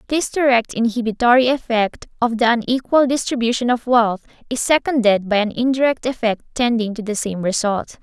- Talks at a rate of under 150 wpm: No, average, 155 wpm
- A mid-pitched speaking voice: No, high, 235 Hz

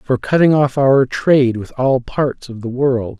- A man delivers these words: Yes, male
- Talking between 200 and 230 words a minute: Yes, fast, 205 wpm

